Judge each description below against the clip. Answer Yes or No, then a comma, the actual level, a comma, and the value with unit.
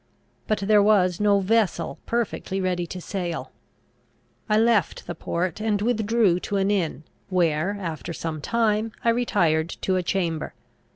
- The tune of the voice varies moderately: Yes, average, 3.8 semitones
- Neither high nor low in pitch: No, high, 195 Hz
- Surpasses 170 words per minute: No, average, 150 wpm